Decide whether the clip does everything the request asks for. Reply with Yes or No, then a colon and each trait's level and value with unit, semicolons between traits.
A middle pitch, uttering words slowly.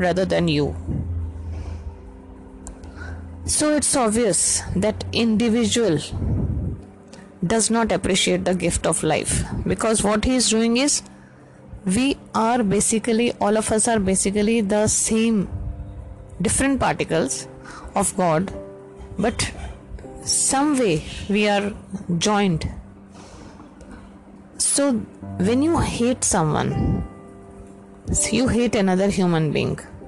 Yes: medium, 180 Hz; slow, 100 wpm